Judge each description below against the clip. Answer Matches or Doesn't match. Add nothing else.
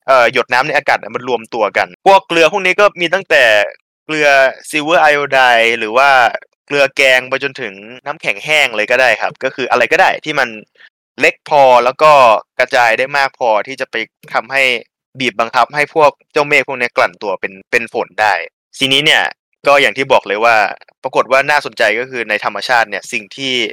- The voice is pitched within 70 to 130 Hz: Doesn't match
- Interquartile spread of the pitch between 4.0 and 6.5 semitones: Doesn't match